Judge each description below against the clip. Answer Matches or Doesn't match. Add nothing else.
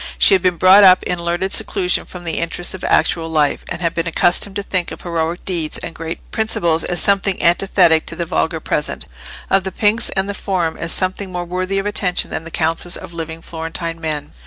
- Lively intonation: Doesn't match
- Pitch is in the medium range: Matches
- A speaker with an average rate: Doesn't match